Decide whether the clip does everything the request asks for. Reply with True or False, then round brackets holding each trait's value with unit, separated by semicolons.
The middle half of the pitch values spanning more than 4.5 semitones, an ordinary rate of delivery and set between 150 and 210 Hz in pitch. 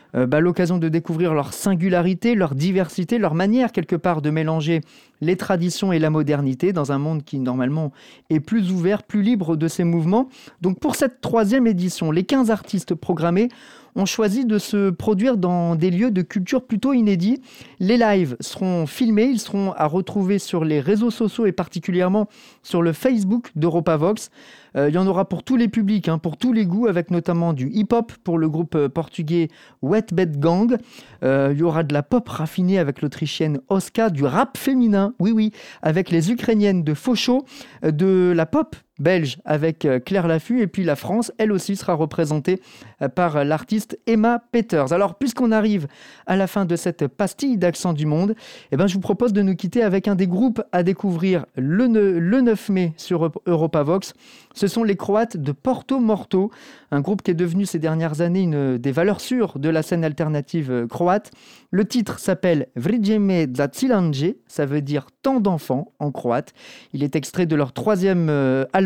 True (5.0 semitones; 185 wpm; 185 Hz)